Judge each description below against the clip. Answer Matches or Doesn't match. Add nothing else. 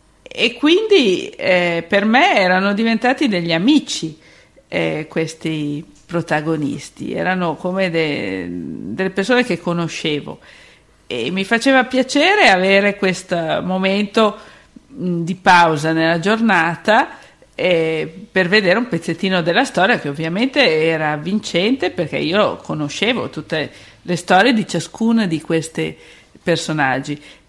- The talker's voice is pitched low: Doesn't match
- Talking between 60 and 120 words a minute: Matches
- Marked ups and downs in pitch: Matches